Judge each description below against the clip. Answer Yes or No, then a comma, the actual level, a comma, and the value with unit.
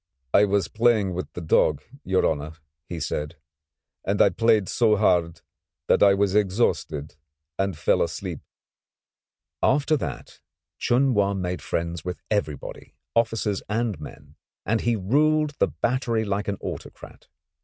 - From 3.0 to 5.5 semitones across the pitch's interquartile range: Yes, average, 4.4 semitones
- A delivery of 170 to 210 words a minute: No, average, 140 wpm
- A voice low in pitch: Yes, low, 100 Hz